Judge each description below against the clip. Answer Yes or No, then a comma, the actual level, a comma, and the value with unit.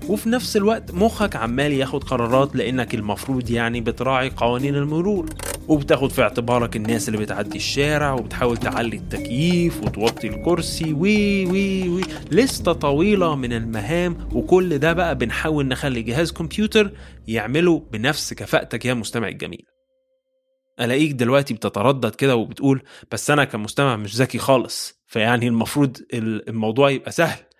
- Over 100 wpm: Yes, fast, 135 wpm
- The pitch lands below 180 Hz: Yes, low, 135 Hz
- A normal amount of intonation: No, wide, 6.2 semitones